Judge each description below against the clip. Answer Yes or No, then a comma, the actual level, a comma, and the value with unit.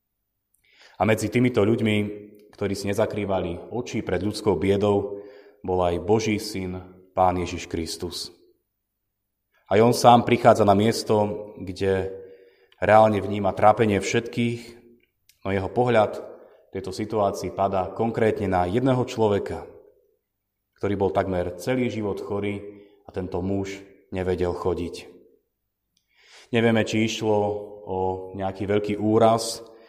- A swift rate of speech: No, average, 115 wpm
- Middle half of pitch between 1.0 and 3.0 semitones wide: Yes, narrow, 2.4 semitones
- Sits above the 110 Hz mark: No, low, 100 Hz